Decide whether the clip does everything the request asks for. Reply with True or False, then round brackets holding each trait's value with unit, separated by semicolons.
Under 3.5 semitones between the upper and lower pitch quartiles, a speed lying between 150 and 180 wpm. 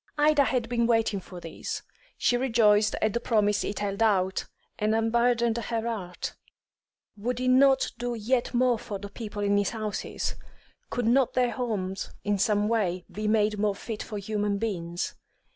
True (2.7 semitones; 175 wpm)